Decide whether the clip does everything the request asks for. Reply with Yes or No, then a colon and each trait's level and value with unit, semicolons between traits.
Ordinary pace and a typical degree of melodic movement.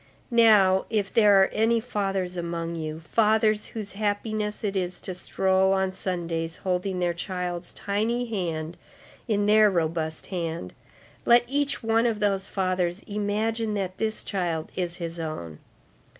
Yes: average, 145 wpm; average, 3.6 semitones